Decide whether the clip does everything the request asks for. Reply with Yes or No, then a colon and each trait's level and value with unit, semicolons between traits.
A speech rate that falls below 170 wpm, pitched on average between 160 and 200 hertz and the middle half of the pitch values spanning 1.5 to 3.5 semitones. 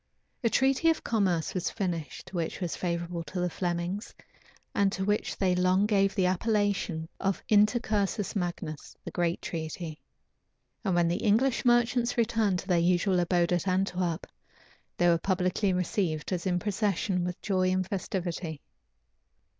Yes: average, 150 wpm; medium, 185 Hz; average, 2.8 semitones